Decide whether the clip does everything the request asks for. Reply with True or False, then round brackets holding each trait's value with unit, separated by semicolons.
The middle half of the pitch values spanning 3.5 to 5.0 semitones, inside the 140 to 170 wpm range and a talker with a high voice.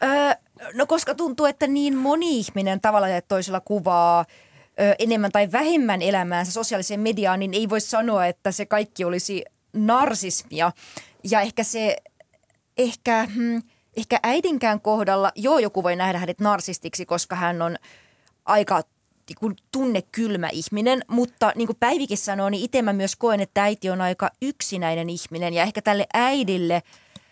True (4.1 semitones; 145 wpm; 210 Hz)